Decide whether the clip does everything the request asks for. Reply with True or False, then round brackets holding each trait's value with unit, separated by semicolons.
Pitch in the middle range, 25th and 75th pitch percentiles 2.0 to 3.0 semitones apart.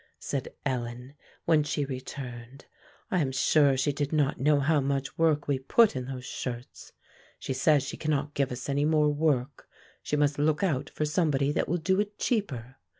True (145 Hz; 2.5 semitones)